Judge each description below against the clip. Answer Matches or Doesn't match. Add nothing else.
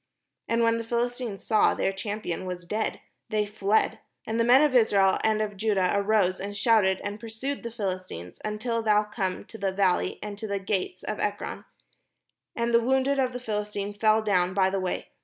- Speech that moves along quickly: Doesn't match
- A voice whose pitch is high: Matches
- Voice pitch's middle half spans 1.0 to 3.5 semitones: Matches